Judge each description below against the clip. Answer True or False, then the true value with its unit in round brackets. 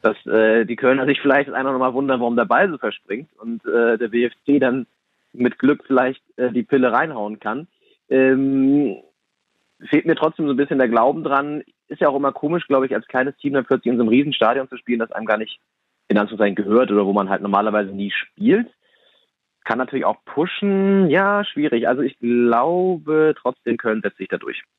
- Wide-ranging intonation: False (3.4 semitones)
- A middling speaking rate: False (210 wpm)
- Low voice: True (130 Hz)